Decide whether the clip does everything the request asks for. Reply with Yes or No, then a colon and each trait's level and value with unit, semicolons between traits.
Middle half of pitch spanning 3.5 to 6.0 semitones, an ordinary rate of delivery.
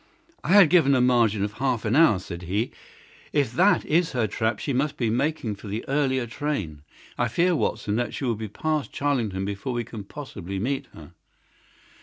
Yes: wide, 5.4 semitones; average, 195 wpm